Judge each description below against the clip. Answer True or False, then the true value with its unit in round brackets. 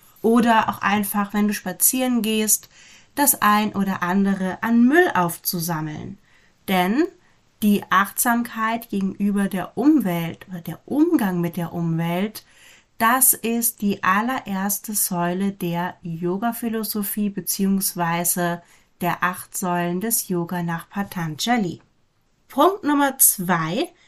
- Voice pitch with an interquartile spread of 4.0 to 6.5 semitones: True (4.3 semitones)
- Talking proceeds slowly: True (110 wpm)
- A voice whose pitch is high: True (200 Hz)